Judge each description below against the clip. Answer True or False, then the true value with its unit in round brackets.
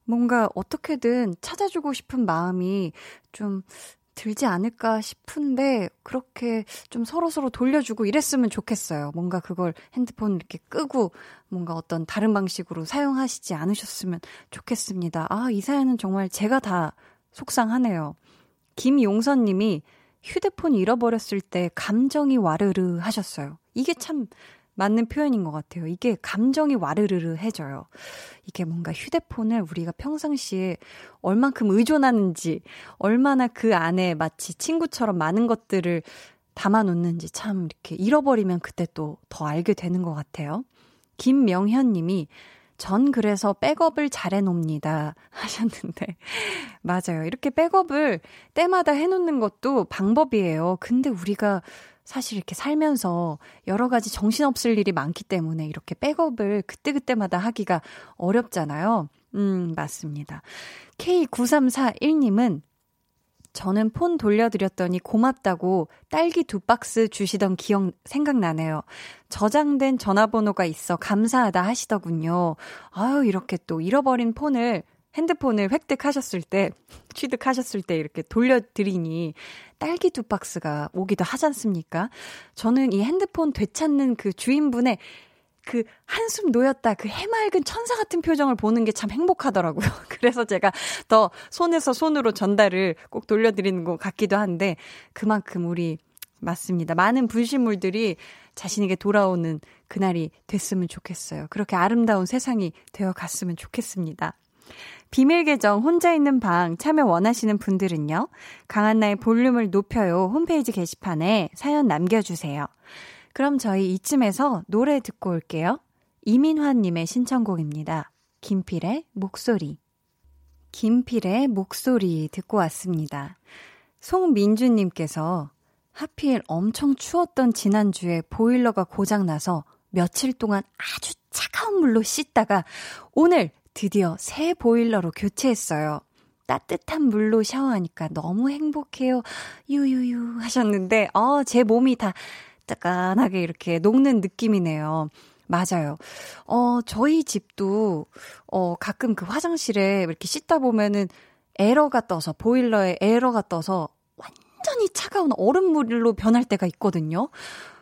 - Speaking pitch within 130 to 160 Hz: False (215 Hz)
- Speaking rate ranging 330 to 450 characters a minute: False (295 characters per minute)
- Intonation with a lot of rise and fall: True (6.1 semitones)